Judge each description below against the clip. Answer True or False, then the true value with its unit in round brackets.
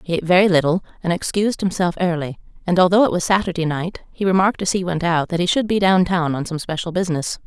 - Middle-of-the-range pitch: True (175 Hz)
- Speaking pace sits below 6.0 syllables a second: False (6.7 syllables/s)